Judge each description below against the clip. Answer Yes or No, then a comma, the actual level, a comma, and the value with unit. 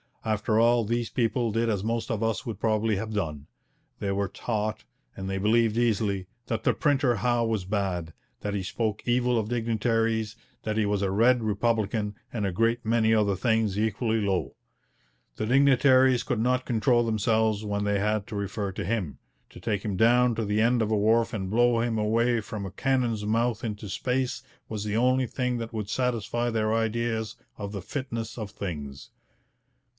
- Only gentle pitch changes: Yes, narrow, 2.3 semitones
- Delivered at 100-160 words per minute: No, average, 185 wpm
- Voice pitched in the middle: No, low, 110 Hz